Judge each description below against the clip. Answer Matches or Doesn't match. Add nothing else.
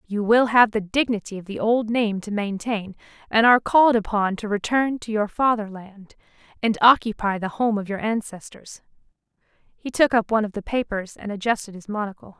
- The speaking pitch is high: Matches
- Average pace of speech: Matches